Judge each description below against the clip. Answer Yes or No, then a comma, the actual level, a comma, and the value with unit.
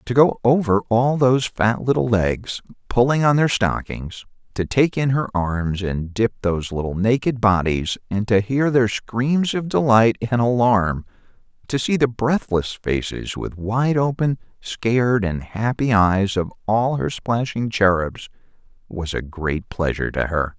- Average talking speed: Yes, average, 160 wpm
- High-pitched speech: No, low, 110 Hz